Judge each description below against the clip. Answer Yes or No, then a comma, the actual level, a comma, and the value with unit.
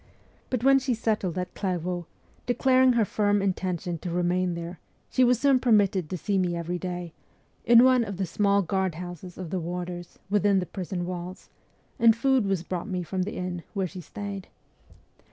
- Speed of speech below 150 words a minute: No, average, 185 wpm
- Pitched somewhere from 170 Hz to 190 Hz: Yes, medium, 185 Hz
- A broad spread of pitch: No, average, 3.1 semitones